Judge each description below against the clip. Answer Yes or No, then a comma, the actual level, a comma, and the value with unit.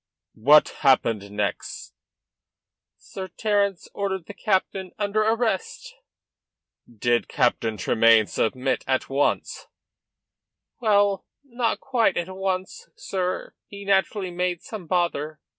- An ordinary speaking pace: No, slow, 105 wpm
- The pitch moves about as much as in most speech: No, wide, 6.4 semitones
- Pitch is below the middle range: No, medium, 185 Hz